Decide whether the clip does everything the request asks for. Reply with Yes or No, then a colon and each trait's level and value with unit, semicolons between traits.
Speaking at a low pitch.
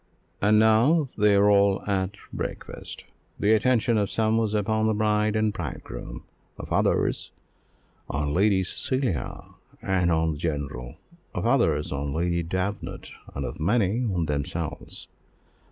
Yes: low, 100 Hz